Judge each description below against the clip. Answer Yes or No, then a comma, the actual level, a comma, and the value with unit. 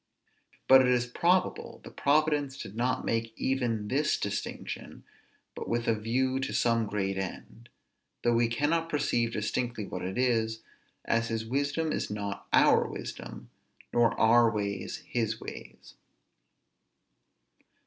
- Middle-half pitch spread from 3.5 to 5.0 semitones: No, average, 2.9 semitones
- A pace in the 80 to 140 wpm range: Yes, slow, 135 wpm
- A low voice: Yes, low, 115 Hz